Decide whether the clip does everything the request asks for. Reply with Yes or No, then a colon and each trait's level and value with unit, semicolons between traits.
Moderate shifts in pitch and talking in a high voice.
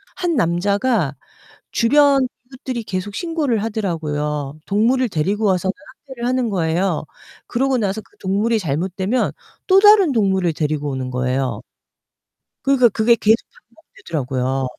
No: wide, 7.9 semitones; high, 200 Hz